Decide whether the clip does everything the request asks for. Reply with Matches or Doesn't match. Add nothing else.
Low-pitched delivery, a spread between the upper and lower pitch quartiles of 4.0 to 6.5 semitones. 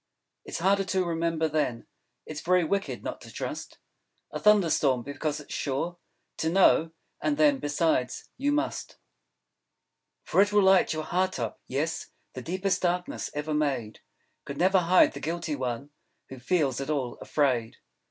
Doesn't match